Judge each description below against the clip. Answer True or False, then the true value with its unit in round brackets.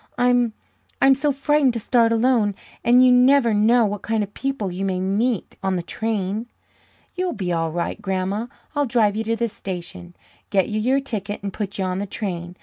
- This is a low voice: False (215 Hz)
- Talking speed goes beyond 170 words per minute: True (200 wpm)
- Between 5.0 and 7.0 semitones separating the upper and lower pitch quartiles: False (4.3 semitones)